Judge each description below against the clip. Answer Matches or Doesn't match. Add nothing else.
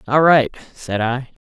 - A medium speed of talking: Matches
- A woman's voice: Doesn't match